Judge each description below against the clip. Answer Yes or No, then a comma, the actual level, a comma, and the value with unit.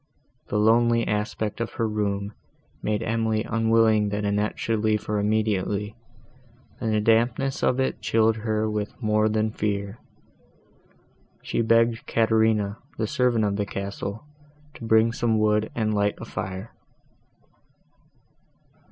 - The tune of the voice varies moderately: No, narrow, 1.4 semitones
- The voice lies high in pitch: No, low, 110 Hz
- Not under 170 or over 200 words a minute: No, slow, 135 wpm